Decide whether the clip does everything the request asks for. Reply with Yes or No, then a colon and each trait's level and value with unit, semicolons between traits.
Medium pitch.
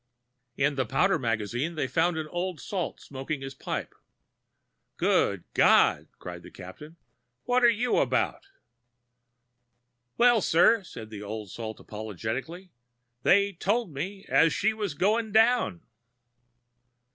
Yes: medium, 165 Hz